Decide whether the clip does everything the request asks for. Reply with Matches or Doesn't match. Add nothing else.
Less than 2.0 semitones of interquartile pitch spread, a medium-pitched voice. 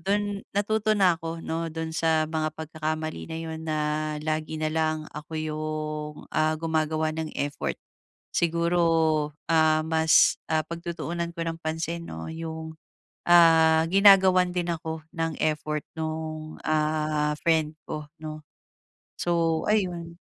Matches